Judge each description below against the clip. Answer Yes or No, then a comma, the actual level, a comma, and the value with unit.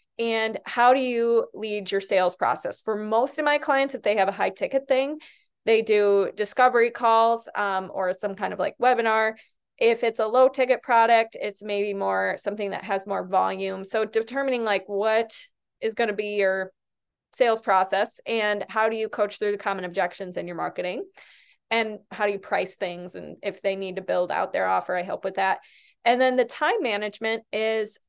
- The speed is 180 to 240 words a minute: Yes, average, 200 wpm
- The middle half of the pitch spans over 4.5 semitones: No, average, 3.0 semitones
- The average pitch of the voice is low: No, high, 215 Hz